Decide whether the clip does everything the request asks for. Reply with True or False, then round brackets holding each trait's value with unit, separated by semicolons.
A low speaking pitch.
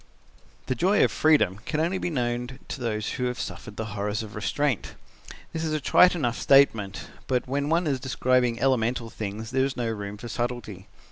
True (125 Hz)